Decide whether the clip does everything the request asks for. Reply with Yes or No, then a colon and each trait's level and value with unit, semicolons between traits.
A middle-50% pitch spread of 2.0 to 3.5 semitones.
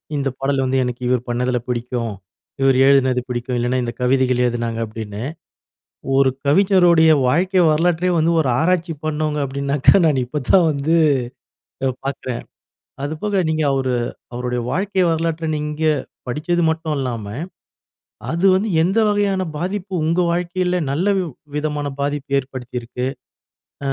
No: average, 5.0 semitones